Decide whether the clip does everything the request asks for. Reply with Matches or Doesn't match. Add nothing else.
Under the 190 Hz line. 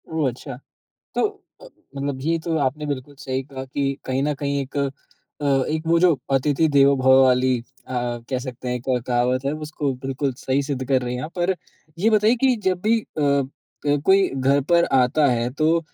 Matches